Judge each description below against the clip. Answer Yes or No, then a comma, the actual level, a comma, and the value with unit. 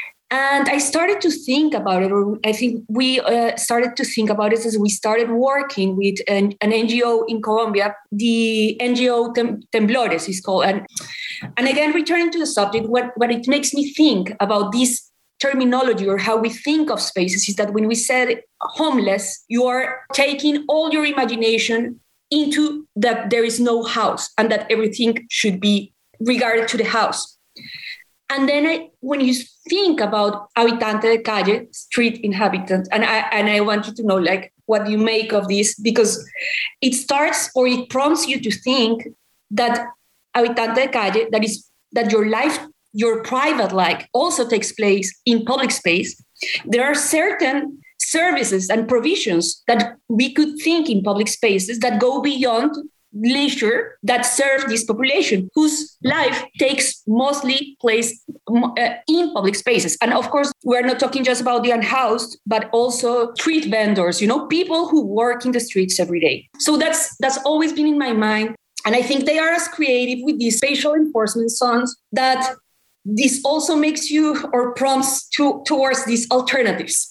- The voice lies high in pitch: Yes, high, 240 Hz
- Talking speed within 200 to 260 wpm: No, average, 170 wpm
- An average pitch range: Yes, average, 4.1 semitones